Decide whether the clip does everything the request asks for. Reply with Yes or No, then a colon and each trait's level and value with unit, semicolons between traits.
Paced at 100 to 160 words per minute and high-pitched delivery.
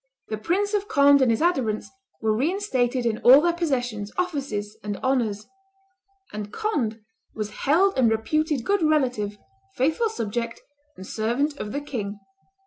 Yes: average, 145 wpm; very high, 255 Hz